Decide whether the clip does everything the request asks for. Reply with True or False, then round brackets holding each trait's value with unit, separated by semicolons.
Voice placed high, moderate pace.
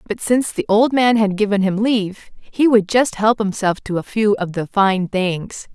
False (210 Hz; 220 wpm)